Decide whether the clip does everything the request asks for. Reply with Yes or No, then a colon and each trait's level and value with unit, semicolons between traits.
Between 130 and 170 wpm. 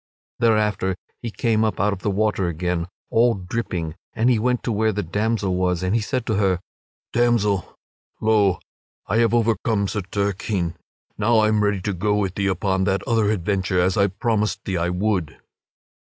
No: average, 180 wpm